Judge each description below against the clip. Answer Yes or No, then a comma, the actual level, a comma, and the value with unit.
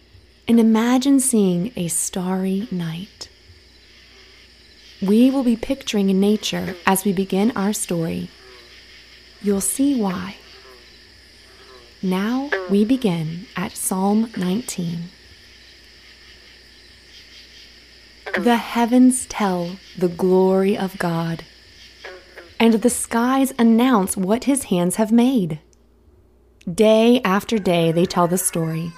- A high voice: Yes, high, 195 Hz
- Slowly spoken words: Yes, slow, 100 wpm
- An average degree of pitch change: Yes, average, 4.5 semitones